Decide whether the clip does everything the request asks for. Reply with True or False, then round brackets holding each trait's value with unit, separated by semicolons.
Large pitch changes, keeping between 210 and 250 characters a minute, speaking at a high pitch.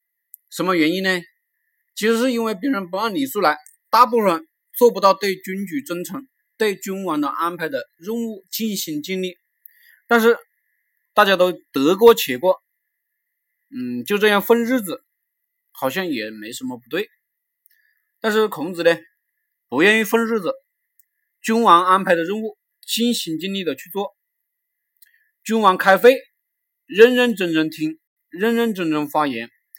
True (5.8 semitones; 215 characters per minute; 215 Hz)